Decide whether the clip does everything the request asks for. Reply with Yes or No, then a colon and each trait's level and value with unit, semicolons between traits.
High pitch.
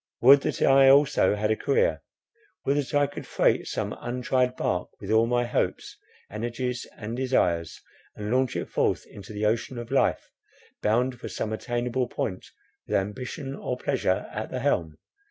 No: low, 120 Hz